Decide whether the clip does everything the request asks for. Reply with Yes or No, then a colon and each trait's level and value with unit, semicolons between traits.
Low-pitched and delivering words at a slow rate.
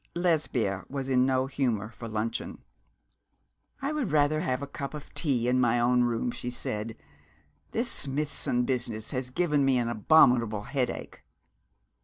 No: low, 125 Hz; average, 150 wpm